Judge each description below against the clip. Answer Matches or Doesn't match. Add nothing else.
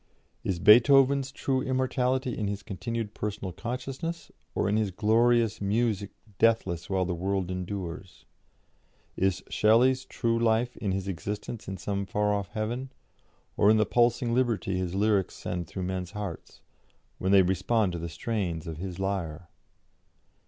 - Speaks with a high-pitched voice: Doesn't match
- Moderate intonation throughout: Matches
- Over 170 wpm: Doesn't match